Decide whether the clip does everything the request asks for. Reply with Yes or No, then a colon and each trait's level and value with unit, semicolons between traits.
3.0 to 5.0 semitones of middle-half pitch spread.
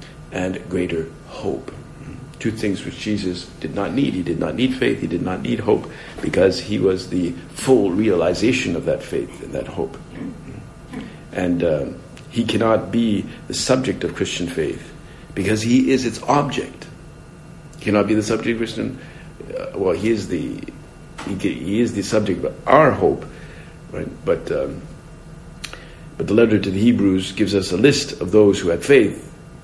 No: wide, 5.5 semitones